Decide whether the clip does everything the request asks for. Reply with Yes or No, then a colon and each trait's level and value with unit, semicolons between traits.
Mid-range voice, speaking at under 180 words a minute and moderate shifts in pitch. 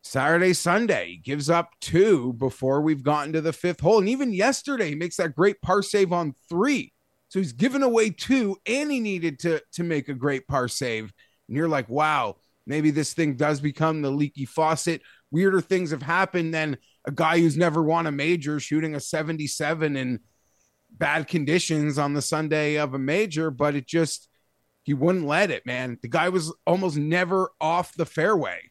No: medium, 160 Hz; average, 190 wpm; average, 3.5 semitones